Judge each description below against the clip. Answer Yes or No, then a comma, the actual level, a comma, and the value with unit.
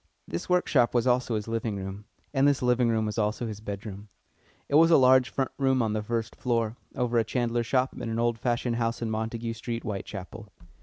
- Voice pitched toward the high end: No, low, 115 Hz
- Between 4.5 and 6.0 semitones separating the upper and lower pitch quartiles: No, narrow, 2.4 semitones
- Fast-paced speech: Yes, fast, 210 wpm